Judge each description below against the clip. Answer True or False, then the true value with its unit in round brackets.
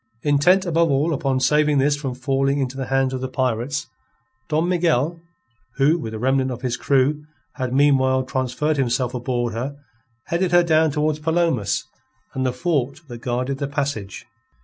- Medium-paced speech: True (170 wpm)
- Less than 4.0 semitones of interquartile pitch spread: True (2.9 semitones)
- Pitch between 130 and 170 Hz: True (135 Hz)